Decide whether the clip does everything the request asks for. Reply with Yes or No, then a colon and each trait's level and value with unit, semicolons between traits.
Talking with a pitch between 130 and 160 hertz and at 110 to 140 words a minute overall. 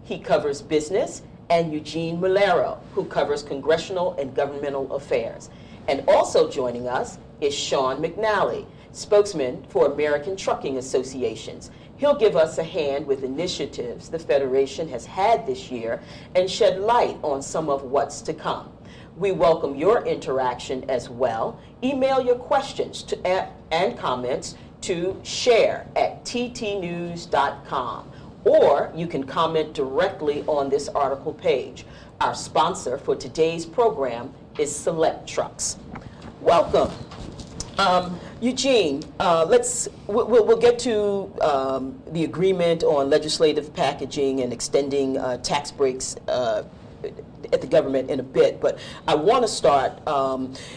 No: medium, 170 Hz; slow, 135 wpm